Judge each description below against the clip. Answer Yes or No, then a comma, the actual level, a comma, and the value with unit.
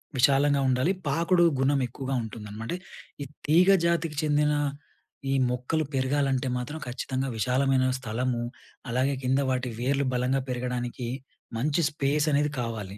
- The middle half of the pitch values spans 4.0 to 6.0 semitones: No, average, 2.7 semitones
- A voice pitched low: Yes, low, 130 Hz